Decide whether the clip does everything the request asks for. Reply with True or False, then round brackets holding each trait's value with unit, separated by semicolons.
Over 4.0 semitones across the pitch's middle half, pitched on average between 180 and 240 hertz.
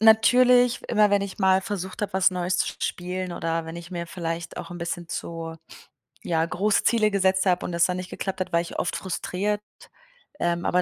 False (2.7 semitones; 185 Hz)